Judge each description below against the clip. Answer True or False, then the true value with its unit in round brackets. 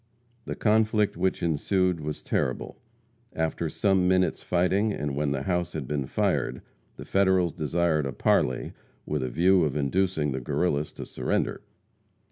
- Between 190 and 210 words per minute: False (150 wpm)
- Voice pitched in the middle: False (85 Hz)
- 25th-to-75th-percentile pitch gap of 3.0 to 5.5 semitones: True (4.2 semitones)